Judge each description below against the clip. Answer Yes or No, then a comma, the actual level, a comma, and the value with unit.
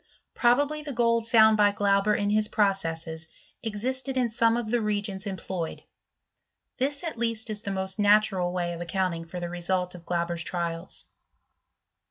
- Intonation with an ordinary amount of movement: Yes, average, 4.4 semitones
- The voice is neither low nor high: No, high, 205 Hz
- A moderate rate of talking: Yes, average, 170 wpm